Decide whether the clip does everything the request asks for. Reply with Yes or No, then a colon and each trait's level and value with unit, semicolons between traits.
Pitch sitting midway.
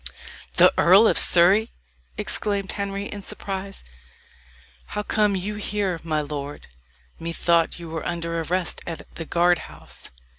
Yes: medium, 175 Hz